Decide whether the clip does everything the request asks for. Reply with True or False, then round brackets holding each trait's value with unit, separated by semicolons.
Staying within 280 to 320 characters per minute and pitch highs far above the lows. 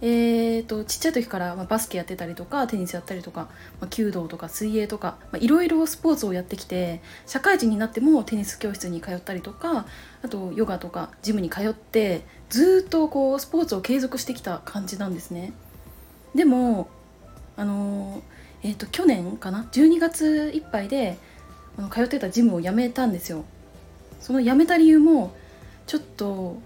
False (345 characters per minute; 6.6 semitones)